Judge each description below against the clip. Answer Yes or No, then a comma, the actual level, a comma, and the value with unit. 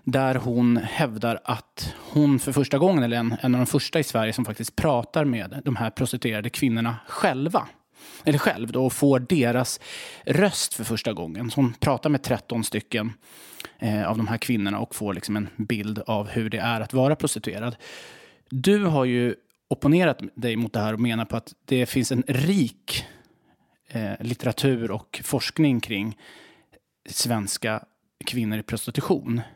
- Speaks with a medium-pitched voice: No, low, 120 Hz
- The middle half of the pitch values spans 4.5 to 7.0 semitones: No, average, 3.4 semitones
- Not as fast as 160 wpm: No, average, 165 wpm